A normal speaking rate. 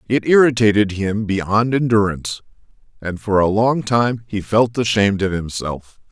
Yes: average, 145 wpm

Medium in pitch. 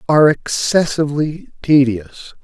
Yes: medium, 145 Hz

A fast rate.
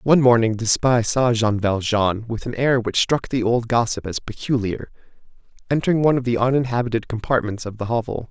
No: average, 190 wpm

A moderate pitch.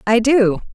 No: high, 235 Hz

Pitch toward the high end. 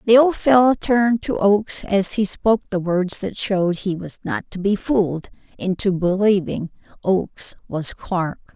Yes: high, 200 Hz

